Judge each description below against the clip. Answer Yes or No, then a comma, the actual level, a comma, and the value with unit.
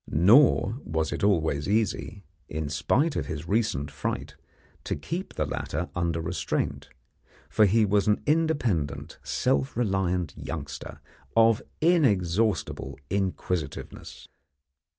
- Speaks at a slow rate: Yes, slow, 110 wpm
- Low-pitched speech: Yes, very low, 95 Hz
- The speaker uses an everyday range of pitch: No, wide, 6.1 semitones